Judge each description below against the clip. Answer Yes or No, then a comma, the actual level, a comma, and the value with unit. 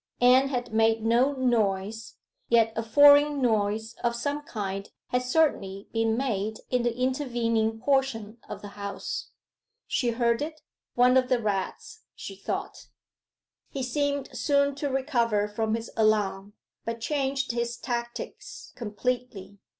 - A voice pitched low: No, high, 235 Hz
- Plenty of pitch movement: No, average, 3.2 semitones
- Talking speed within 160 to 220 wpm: No, slow, 135 wpm